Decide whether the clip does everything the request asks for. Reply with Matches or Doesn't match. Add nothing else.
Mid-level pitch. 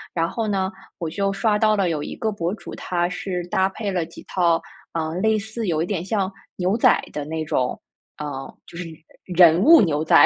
Matches